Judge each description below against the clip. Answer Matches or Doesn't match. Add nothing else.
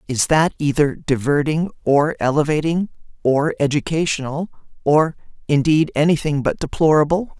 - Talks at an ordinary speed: Doesn't match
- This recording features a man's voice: Doesn't match